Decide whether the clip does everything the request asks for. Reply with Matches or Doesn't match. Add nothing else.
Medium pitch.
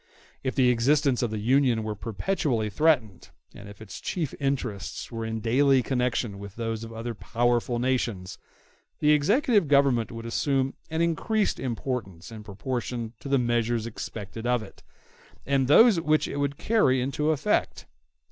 Doesn't match